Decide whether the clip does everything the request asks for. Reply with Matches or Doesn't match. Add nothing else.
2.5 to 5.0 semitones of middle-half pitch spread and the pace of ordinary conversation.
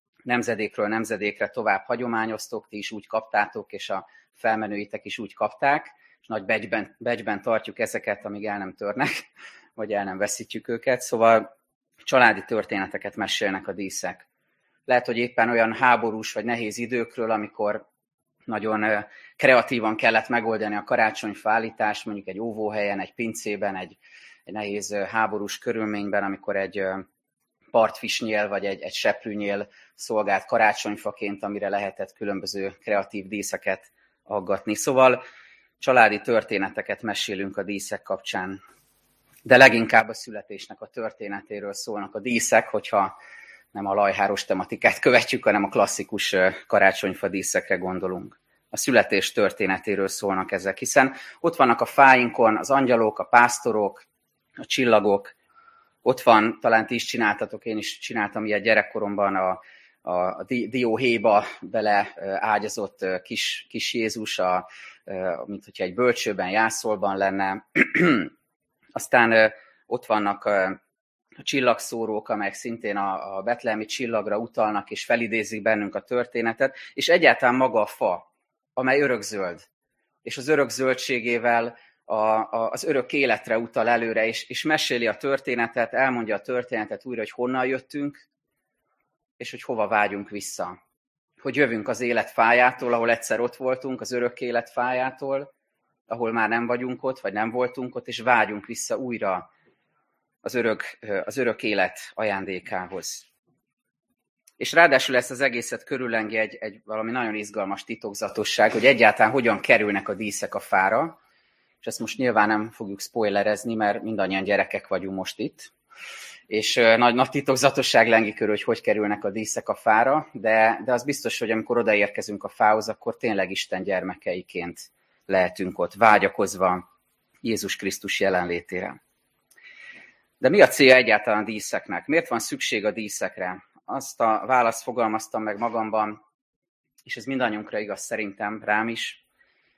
Matches